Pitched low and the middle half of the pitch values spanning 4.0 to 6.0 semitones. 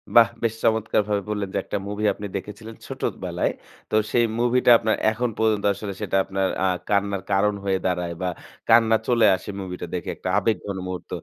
No: low, 105 Hz; narrow, 2.5 semitones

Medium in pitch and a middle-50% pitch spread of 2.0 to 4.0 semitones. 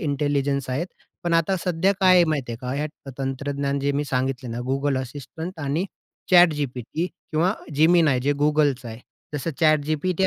Yes: medium, 145 Hz; average, 3.3 semitones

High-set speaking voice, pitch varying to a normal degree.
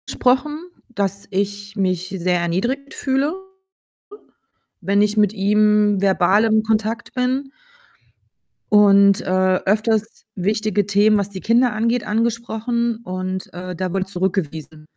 Yes: high, 210 Hz; average, 3.1 semitones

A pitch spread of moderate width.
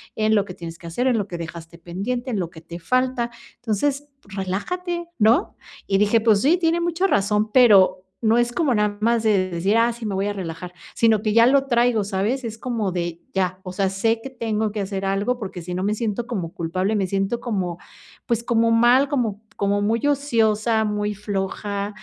Yes: average, 3.7 semitones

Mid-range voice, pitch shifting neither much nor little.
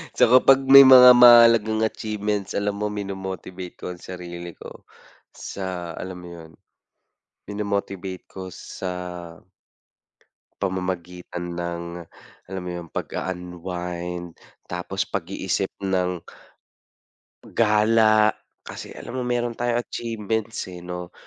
No: very low, 95 Hz; average, 3.5 semitones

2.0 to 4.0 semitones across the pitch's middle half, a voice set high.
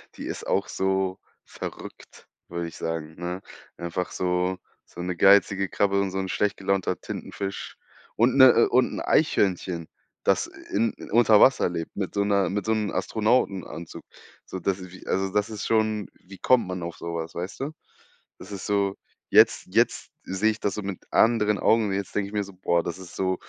No: narrow, 2.5 semitones; very low, 95 Hz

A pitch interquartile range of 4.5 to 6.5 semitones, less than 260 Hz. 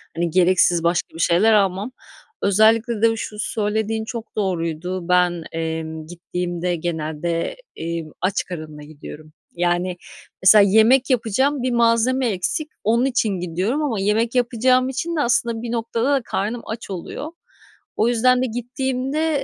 Yes: wide, 5.5 semitones; high, 215 Hz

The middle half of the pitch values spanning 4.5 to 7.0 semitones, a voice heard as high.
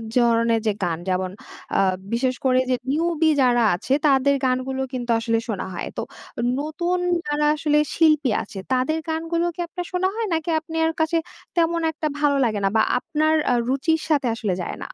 Yes: average, 4.9 semitones; very high, 285 Hz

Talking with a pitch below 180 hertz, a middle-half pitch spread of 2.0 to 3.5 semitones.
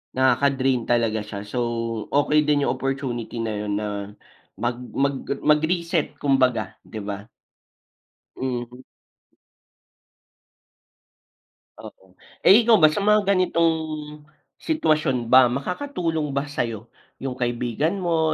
No: low, 135 Hz; average, 4.9 semitones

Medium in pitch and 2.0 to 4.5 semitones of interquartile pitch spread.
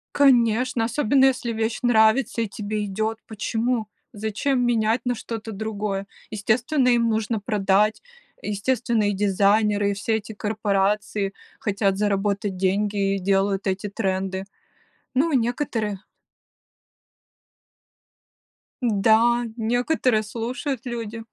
No: high, 220 Hz; average, 2.8 semitones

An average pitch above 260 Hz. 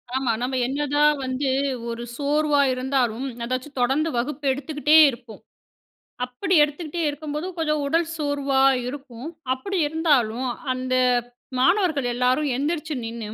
Yes: very high, 280 Hz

